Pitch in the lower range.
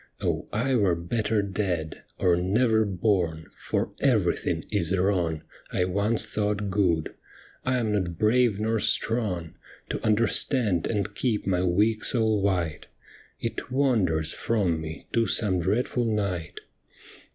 Yes: low, 100 Hz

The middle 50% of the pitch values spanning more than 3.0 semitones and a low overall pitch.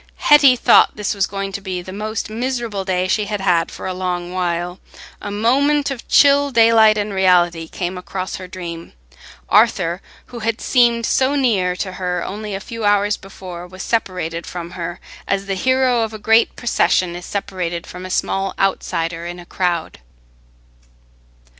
No: average, 3.8 semitones; high, 195 Hz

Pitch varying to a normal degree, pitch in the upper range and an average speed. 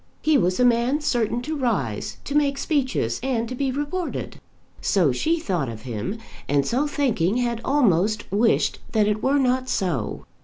No: wide, 6.8 semitones; high, 235 Hz; average, 170 wpm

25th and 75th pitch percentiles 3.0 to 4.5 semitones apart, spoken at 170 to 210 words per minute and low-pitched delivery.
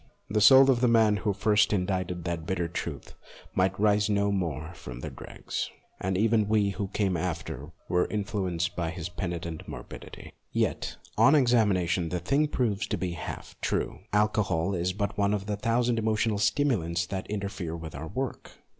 Yes: average, 3.6 semitones; average, 180 wpm; low, 100 Hz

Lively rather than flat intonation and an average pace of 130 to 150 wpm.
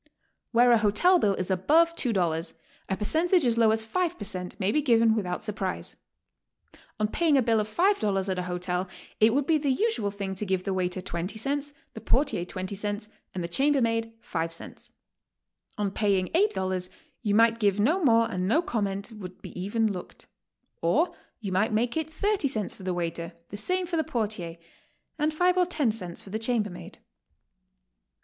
No: wide, 6.7 semitones; average, 185 wpm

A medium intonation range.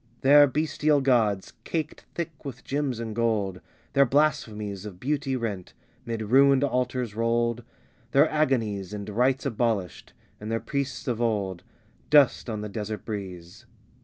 Yes: average, 4.7 semitones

